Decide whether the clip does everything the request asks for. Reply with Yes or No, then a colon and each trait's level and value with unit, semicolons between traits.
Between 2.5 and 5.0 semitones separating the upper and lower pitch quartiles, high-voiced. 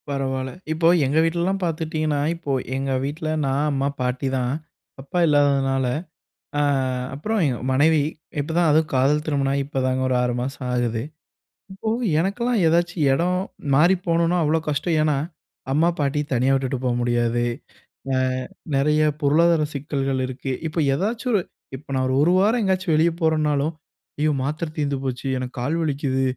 No: average, 3.5 semitones; medium, 145 Hz